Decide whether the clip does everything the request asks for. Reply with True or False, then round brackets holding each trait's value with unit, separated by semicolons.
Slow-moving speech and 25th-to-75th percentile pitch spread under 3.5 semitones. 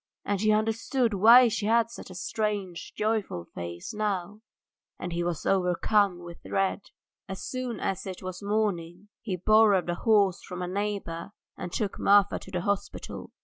False (165 wpm; 3.1 semitones)